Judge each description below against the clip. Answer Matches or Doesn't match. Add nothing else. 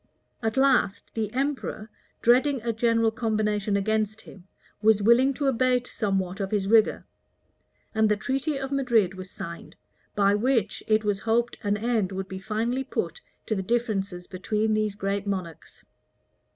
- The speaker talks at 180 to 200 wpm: Doesn't match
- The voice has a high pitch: Matches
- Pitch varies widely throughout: Doesn't match